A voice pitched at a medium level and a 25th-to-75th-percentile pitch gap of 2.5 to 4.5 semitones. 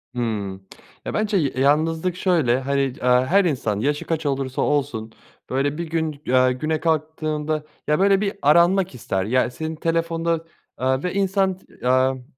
Yes: medium, 150 Hz; average, 4.2 semitones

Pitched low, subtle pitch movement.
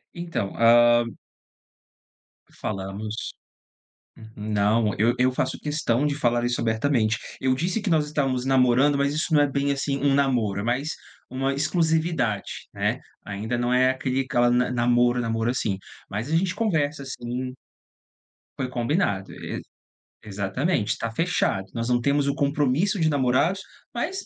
No: low, 130 Hz; average, 3.8 semitones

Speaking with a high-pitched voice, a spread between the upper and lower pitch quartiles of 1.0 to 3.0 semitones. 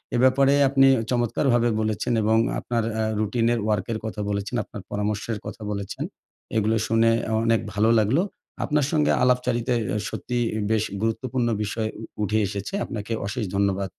No: low, 115 Hz; average, 2.7 semitones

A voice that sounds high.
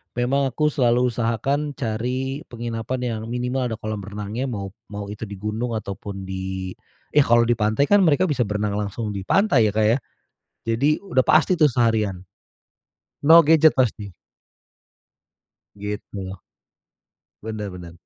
No: low, 115 Hz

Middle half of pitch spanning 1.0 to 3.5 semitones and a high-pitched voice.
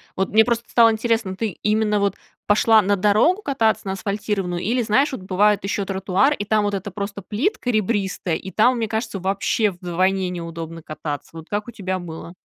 Yes: average, 3.0 semitones; high, 205 Hz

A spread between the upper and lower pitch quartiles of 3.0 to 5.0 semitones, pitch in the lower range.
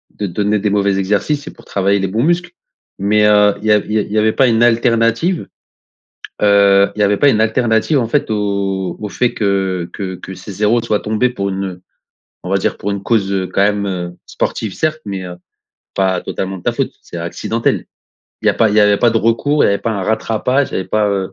No: narrow, 2.6 semitones; low, 105 Hz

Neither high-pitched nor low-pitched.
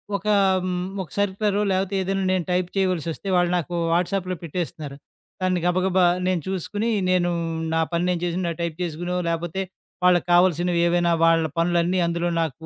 Yes: medium, 175 Hz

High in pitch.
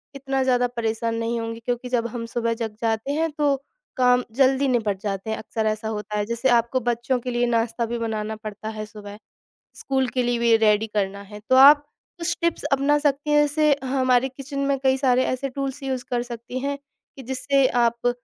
Yes: high, 245 Hz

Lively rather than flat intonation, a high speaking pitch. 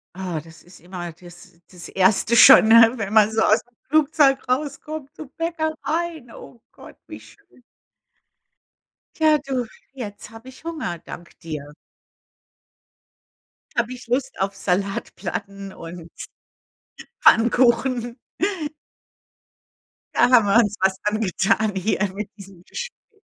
Yes: wide, 5.8 semitones; high, 220 Hz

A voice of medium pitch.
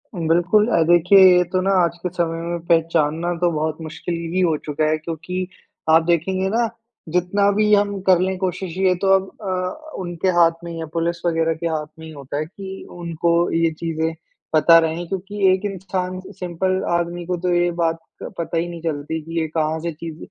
Yes: medium, 170 Hz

